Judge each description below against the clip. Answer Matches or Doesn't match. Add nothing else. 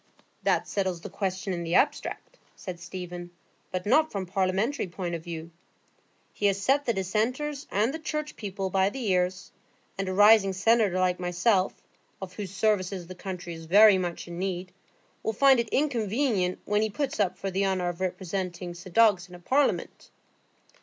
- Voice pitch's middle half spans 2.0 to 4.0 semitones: Matches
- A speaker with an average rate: Matches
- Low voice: Doesn't match